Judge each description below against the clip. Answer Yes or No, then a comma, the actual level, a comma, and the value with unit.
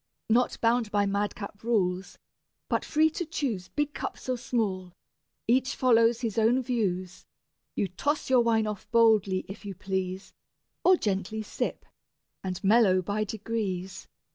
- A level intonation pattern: No, average, 3.9 semitones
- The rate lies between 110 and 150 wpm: Yes, average, 145 wpm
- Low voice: No, high, 215 Hz